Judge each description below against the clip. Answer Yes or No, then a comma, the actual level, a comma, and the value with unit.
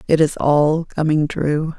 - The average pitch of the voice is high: No, medium, 155 Hz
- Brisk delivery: No, average, 170 wpm